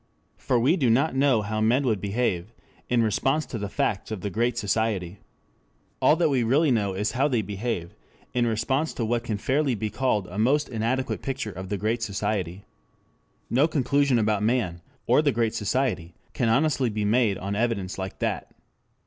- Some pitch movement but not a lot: Yes, average, 4.2 semitones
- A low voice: Yes, low, 115 Hz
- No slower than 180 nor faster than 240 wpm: Yes, average, 185 wpm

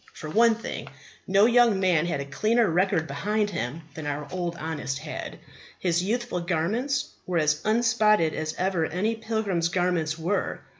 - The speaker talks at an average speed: Yes, average, 155 wpm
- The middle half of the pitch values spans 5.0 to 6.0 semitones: Yes, average, 5.3 semitones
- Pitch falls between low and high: Yes, medium, 180 Hz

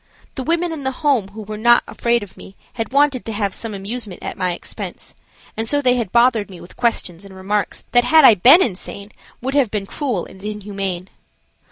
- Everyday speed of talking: No, fast, 210 wpm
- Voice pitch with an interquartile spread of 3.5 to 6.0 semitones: Yes, average, 4.3 semitones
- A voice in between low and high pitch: No, high, 220 Hz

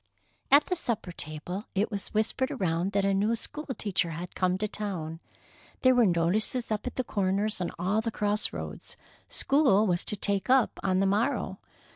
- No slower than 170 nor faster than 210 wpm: Yes, average, 185 wpm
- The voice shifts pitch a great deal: No, average, 3.8 semitones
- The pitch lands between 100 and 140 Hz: No, high, 205 Hz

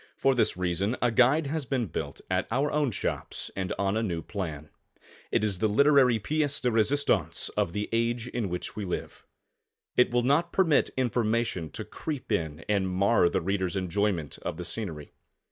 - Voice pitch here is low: Yes, low, 110 Hz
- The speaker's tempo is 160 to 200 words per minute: Yes, average, 180 wpm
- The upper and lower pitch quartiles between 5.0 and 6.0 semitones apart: Yes, wide, 5.5 semitones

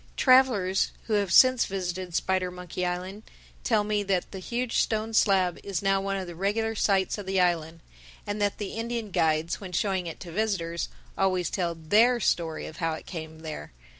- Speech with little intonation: No, average, 3.1 semitones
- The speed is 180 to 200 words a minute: Yes, average, 185 wpm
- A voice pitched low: No, high, 190 Hz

